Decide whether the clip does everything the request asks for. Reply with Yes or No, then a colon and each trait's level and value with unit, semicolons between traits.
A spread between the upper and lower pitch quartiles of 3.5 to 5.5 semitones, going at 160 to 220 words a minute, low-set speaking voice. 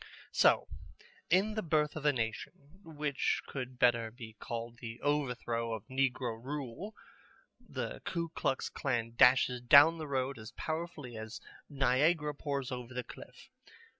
No: average, 3.9 semitones; average, 140 wpm; low, 130 Hz